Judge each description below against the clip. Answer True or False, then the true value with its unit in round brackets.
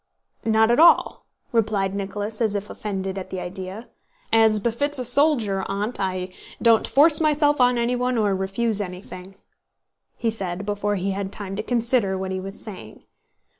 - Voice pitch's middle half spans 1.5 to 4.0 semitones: True (3.5 semitones)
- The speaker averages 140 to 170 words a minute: True (165 wpm)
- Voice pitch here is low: False (210 Hz)